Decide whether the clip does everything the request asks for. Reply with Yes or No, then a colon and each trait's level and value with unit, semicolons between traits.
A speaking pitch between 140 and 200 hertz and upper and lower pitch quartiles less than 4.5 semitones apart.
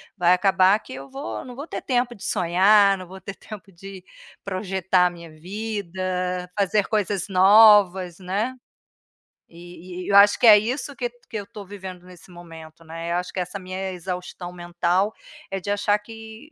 Yes: high, 190 Hz; narrow, 2.6 semitones